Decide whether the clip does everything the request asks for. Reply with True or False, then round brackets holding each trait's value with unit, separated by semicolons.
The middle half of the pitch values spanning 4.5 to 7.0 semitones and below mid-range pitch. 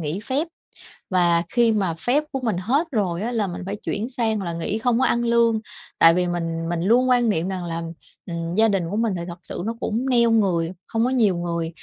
False (5.3 semitones; 205 Hz)